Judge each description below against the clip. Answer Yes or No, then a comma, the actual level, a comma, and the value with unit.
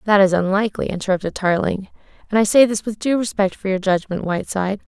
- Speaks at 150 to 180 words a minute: No, average, 195 wpm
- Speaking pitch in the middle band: No, high, 200 Hz